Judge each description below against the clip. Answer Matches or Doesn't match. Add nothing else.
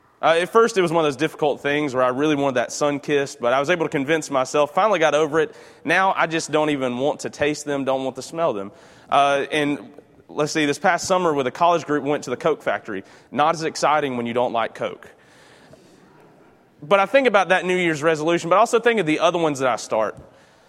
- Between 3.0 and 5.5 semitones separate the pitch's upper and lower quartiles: Matches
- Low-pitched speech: Doesn't match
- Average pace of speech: Doesn't match